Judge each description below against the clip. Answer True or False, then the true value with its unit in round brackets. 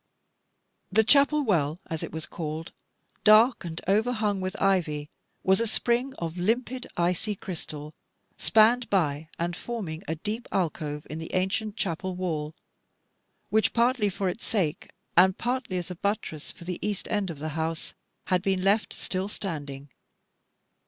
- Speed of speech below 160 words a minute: True (150 wpm)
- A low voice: False (185 Hz)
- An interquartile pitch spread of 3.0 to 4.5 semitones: False (4.9 semitones)